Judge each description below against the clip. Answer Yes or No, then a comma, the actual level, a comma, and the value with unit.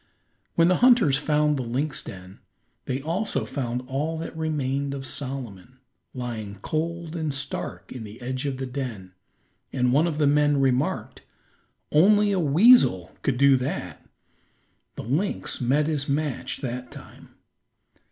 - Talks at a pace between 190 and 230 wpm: No, average, 145 wpm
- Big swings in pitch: No, average, 3.8 semitones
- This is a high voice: No, medium, 140 Hz